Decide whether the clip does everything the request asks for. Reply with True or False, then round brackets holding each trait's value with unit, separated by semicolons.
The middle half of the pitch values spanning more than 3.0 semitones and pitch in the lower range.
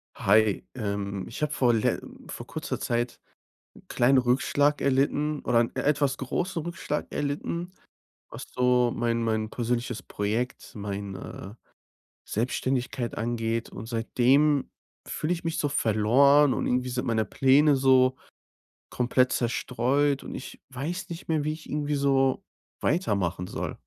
True (3.9 semitones; 125 Hz)